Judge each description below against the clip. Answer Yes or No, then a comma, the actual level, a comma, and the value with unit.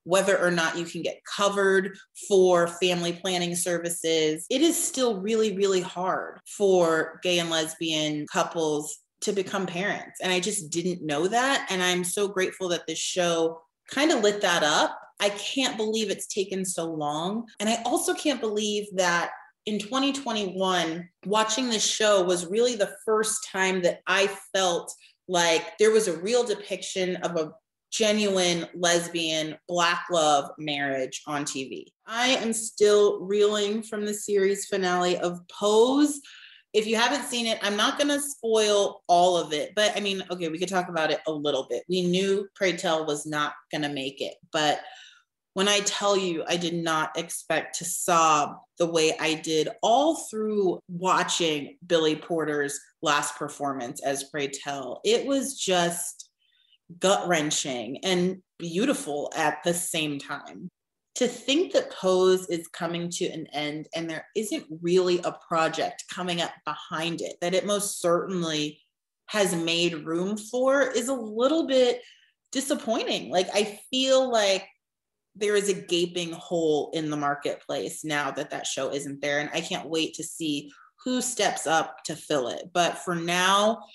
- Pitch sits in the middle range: Yes, medium, 180 Hz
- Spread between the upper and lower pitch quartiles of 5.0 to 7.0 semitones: No, average, 4.3 semitones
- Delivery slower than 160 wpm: No, average, 165 wpm